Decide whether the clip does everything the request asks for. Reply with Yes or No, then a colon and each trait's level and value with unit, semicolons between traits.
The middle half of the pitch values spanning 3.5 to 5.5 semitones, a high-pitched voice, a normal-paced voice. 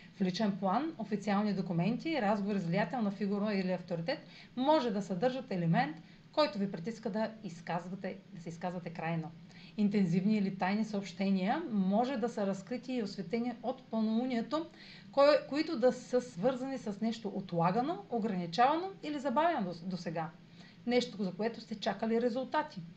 Yes: average, 4.8 semitones; high, 205 Hz; average, 140 wpm